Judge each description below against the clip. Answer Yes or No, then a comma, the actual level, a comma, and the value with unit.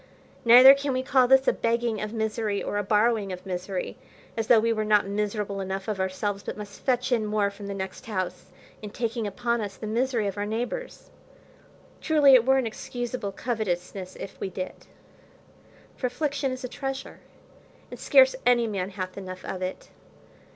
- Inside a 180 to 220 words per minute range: Yes, average, 185 wpm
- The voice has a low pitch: No, high, 215 Hz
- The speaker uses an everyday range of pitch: Yes, average, 3.8 semitones